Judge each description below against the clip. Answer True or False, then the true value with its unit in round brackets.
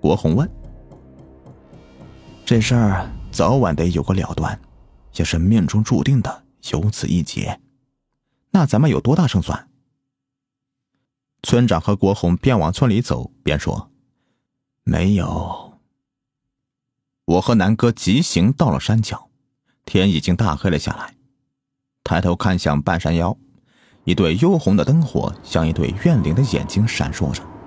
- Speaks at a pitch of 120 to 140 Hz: False (105 Hz)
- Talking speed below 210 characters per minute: True (195 characters per minute)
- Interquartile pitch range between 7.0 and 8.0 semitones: True (7.6 semitones)